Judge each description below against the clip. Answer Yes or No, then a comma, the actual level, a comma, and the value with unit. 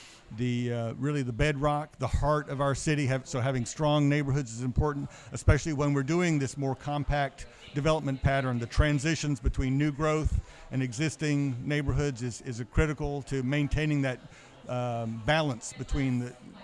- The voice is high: No, medium, 140 Hz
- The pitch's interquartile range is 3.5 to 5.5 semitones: No, average, 2.7 semitones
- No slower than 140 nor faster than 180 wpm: Yes, average, 160 wpm